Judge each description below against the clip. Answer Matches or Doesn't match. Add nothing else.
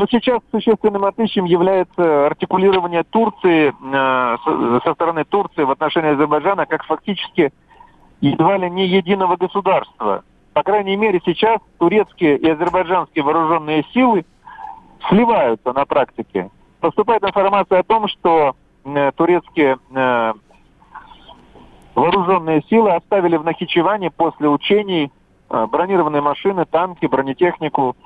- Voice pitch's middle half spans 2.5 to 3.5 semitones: Doesn't match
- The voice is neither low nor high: Matches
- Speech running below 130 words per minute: Matches